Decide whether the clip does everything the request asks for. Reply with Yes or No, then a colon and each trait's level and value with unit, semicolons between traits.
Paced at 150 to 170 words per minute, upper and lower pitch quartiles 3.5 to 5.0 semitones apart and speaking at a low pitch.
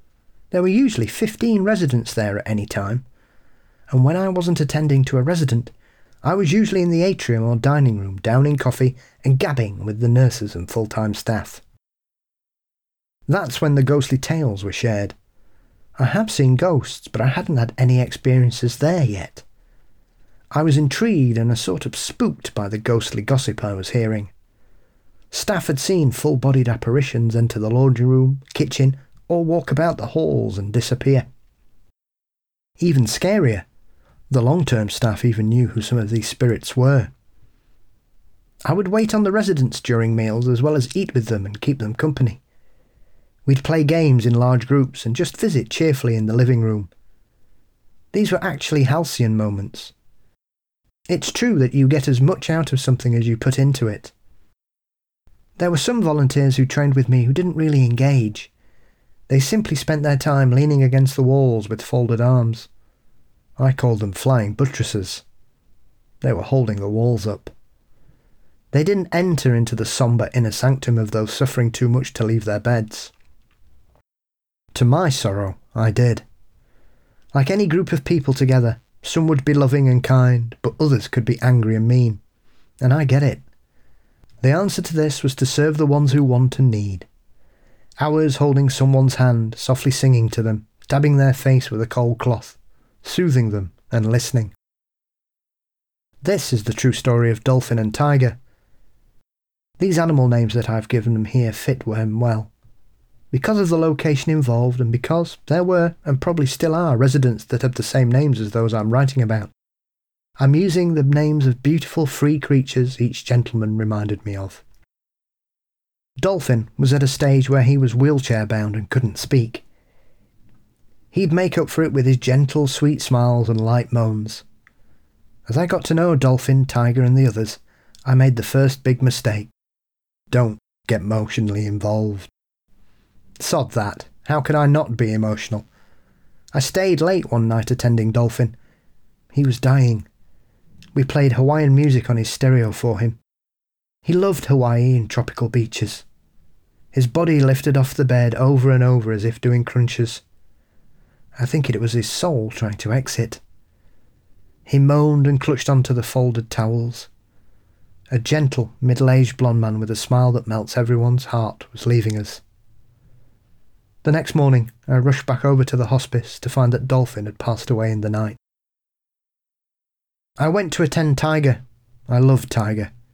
Yes: average, 165 wpm; average, 3.8 semitones; low, 125 Hz